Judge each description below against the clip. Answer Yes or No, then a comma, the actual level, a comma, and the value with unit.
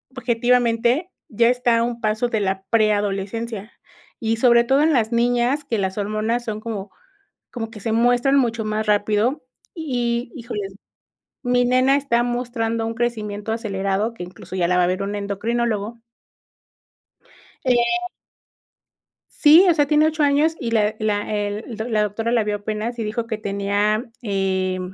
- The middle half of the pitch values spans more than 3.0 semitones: No, average, 2.7 semitones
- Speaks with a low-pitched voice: No, high, 225 Hz